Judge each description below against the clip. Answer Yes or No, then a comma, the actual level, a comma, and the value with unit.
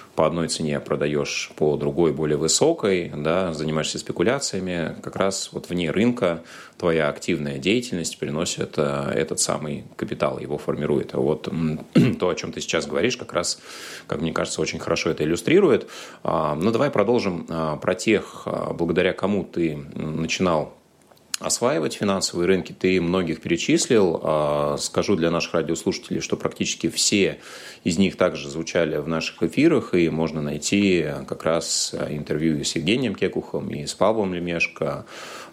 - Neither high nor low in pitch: No, very low, 80 Hz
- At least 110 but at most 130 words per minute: No, average, 140 wpm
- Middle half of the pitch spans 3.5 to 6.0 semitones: No, average, 3.1 semitones